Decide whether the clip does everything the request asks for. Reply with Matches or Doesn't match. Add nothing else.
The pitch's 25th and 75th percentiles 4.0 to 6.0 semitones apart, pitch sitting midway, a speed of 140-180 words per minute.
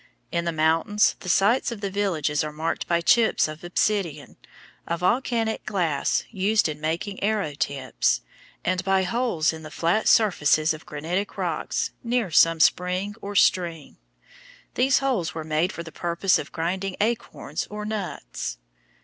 Matches